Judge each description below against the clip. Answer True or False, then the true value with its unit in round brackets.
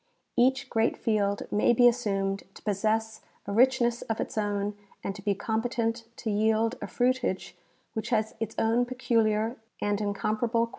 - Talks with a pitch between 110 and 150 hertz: False (220 Hz)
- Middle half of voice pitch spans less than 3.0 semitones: True (2.5 semitones)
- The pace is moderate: True (160 wpm)